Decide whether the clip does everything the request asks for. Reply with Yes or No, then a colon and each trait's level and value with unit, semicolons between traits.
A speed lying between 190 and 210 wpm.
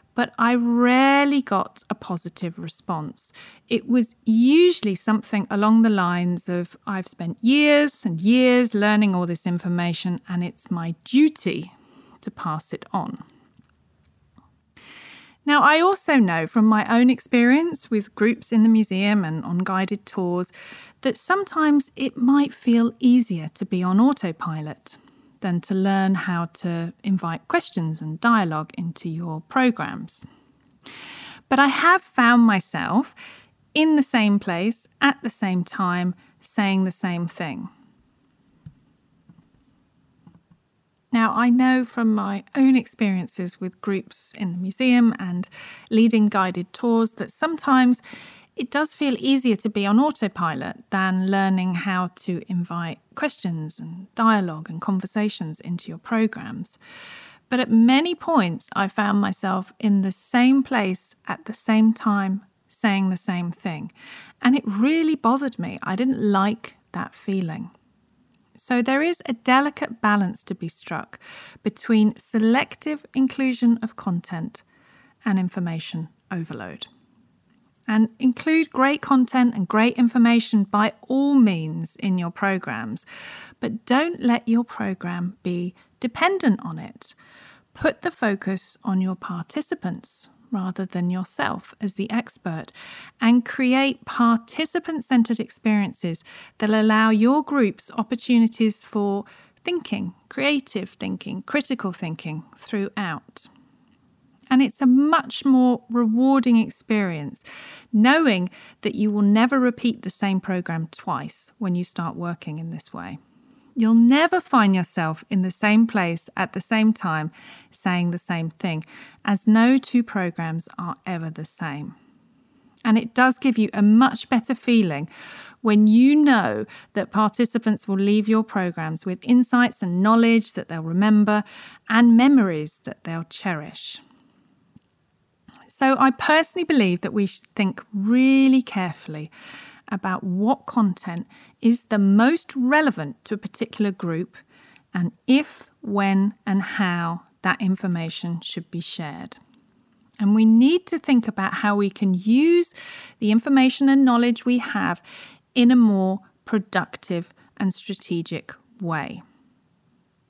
No: slow, 135 wpm